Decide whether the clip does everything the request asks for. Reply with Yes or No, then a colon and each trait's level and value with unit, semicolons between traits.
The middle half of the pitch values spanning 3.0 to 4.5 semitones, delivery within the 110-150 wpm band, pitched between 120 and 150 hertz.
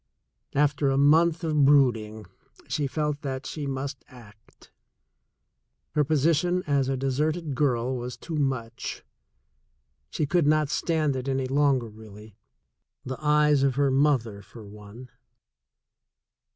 Yes: average, 3.4 semitones; slow, 135 wpm; low, 135 Hz